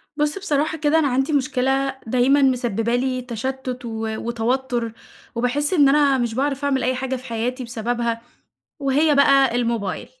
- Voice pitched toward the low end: No, very high, 260 Hz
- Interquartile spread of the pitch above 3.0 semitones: No, average, 2.7 semitones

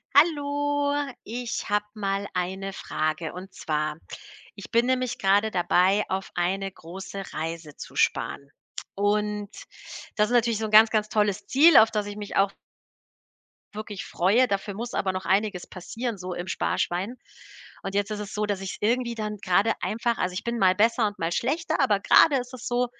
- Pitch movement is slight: No, average, 3.7 semitones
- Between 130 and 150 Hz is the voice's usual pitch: No, high, 210 Hz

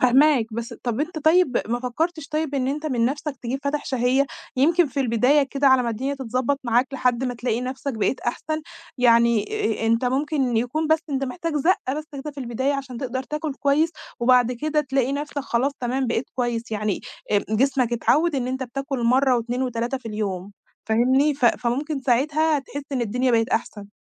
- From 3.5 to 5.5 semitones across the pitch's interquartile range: No, average, 3.1 semitones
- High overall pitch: Yes, very high, 260 Hz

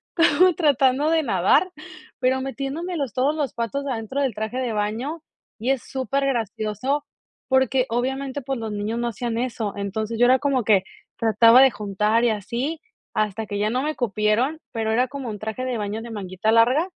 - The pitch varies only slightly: No, average, 3.8 semitones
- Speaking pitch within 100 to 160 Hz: No, high, 245 Hz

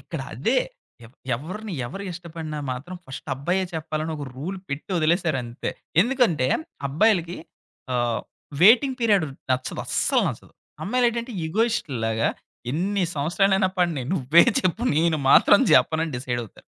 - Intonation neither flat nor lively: No, wide, 5.9 semitones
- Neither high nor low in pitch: Yes, medium, 165 Hz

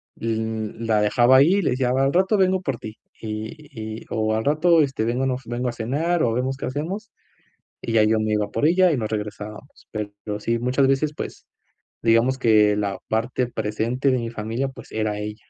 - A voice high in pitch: No, low, 120 Hz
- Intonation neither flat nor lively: Yes, average, 3.9 semitones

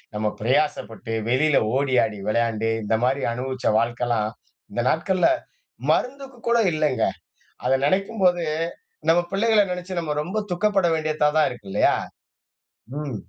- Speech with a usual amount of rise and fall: No, wide, 7.6 semitones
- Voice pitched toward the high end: No, medium, 150 Hz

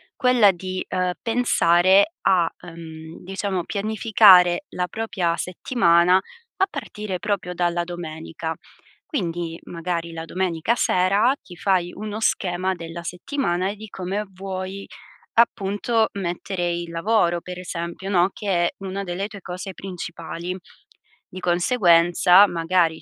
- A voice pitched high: No, medium, 180 Hz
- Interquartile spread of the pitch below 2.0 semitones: No, narrow, 2.6 semitones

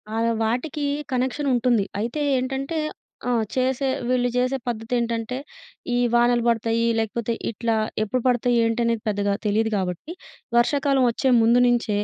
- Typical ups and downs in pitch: No, narrow, 2.0 semitones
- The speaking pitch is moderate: No, high, 240 Hz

